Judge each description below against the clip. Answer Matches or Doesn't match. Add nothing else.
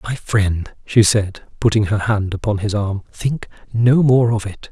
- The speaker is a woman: Doesn't match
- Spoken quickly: Doesn't match